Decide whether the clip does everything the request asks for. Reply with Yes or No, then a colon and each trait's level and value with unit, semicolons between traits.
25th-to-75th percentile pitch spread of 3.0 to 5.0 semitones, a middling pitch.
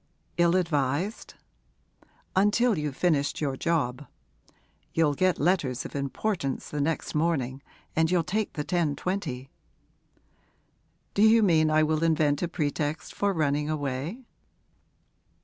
Yes: average, 3.9 semitones; medium, 155 Hz